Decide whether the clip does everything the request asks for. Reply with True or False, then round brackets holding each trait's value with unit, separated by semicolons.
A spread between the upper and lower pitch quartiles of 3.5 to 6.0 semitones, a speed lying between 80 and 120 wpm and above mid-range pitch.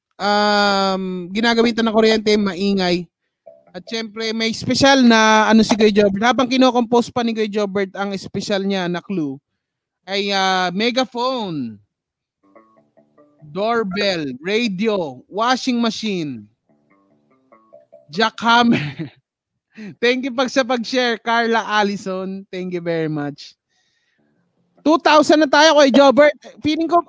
True (5.1 semitones; 115 wpm; 210 Hz)